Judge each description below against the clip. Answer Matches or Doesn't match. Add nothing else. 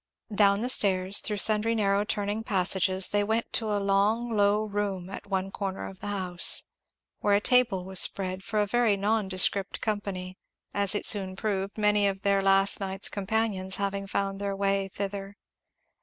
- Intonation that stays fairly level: Matches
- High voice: Matches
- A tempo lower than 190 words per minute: Matches